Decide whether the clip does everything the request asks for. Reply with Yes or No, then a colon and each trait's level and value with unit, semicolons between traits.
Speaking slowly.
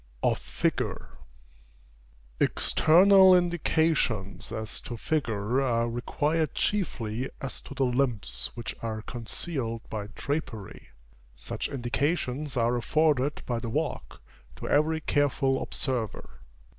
Yes: slow, 105 wpm